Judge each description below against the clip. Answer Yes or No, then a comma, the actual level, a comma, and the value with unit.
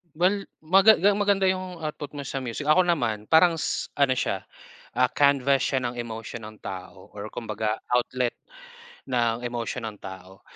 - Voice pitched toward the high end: No, low, 125 Hz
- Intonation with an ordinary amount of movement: No, wide, 6.4 semitones